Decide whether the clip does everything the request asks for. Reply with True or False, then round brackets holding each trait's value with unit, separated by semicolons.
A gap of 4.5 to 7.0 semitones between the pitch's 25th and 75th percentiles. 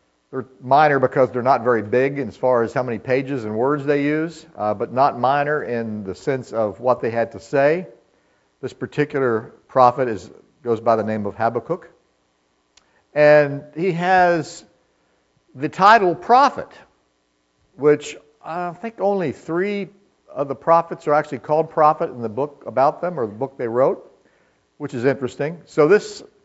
True (5.3 semitones)